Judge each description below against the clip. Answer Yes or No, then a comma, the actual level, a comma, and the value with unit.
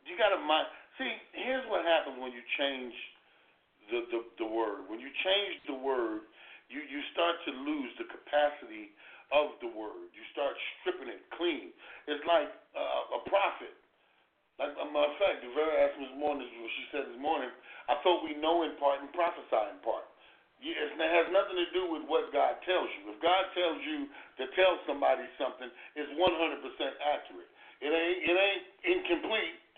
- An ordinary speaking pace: Yes, average, 185 wpm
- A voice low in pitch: No, medium, 175 Hz